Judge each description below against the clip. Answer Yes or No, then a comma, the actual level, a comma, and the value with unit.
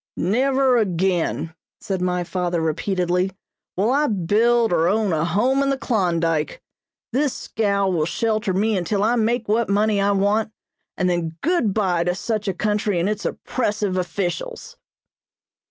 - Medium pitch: No, high, 200 Hz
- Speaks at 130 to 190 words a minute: Yes, average, 155 wpm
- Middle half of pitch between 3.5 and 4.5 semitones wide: Yes, average, 3.9 semitones